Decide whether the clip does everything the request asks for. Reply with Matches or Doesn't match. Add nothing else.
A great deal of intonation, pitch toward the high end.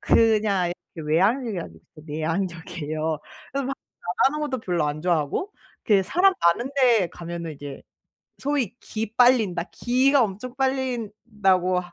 Matches